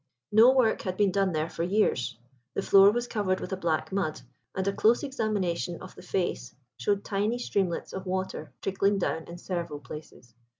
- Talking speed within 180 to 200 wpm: Yes, average, 185 wpm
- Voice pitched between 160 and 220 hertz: Yes, high, 190 Hz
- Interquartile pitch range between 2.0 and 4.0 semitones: Yes, average, 3.1 semitones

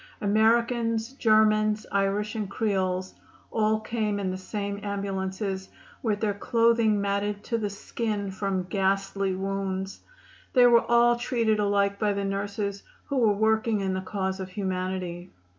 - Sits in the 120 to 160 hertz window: No, high, 205 Hz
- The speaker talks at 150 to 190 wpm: No, average, 140 wpm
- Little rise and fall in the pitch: Yes, narrow, 2.1 semitones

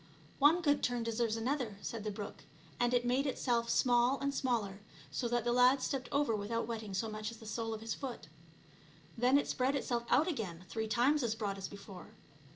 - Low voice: No, high, 235 Hz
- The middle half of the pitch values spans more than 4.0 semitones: No, average, 2.9 semitones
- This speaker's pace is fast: Yes, fast, 210 wpm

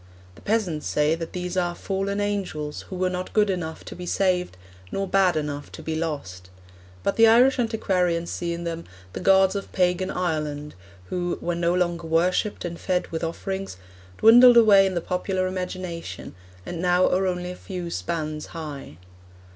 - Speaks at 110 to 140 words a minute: No, average, 175 wpm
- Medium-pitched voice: Yes, medium, 180 Hz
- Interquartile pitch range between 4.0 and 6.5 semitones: No, narrow, 2.5 semitones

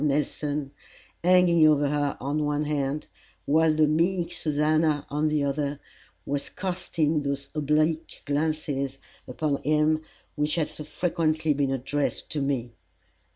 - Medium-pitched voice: Yes, medium, 150 Hz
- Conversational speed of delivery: No, slow, 130 wpm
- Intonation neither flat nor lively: No, narrow, 1.6 semitones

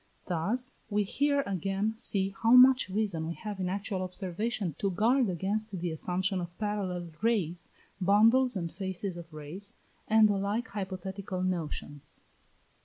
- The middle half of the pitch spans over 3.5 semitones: No, average, 3.2 semitones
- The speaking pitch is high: Yes, high, 195 Hz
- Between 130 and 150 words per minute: Yes, average, 145 wpm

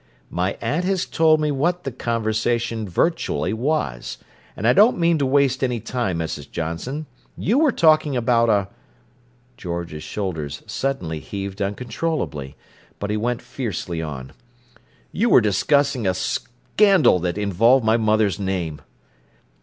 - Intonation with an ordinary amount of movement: No, wide, 7.2 semitones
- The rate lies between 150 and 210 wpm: No, average, 140 wpm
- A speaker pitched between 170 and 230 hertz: No, low, 115 Hz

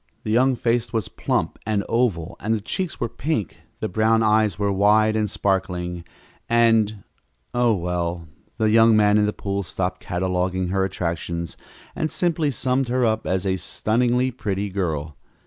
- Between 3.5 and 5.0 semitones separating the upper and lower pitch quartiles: Yes, average, 3.8 semitones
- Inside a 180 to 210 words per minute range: No, average, 165 wpm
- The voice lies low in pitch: Yes, low, 105 Hz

